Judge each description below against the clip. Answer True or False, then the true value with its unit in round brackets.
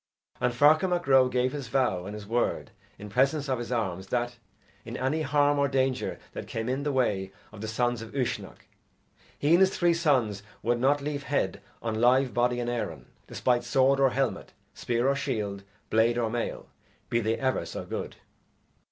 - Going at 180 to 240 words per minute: True (190 wpm)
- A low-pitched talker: True (125 Hz)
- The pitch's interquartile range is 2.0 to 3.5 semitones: True (3.1 semitones)